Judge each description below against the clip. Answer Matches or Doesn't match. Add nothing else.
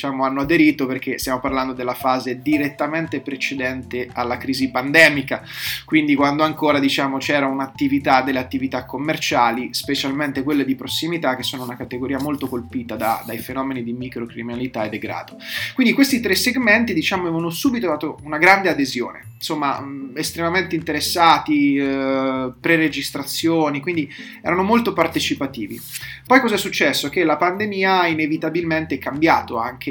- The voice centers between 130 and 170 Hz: Matches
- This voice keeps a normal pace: Matches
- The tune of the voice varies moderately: Matches